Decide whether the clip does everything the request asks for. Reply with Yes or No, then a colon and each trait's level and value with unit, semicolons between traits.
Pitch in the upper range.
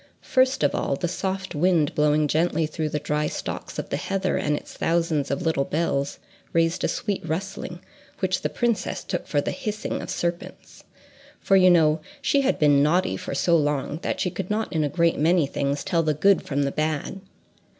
No: medium, 165 Hz